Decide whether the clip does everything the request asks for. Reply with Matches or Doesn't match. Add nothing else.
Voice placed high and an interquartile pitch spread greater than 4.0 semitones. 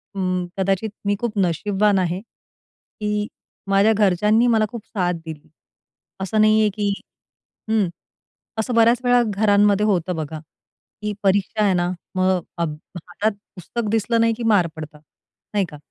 Doesn't match